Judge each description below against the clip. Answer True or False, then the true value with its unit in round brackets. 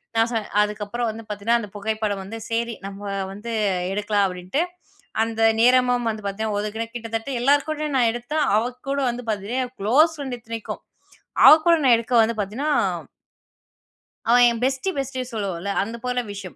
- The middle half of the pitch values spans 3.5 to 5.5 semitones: False (3.0 semitones)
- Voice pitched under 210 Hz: False (230 Hz)